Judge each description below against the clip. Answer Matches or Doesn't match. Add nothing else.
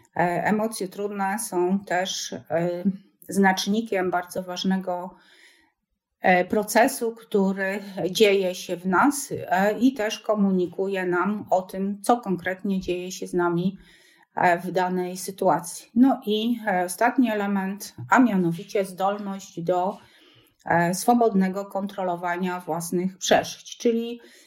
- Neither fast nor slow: Doesn't match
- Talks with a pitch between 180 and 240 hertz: Matches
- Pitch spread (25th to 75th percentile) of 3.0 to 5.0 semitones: Doesn't match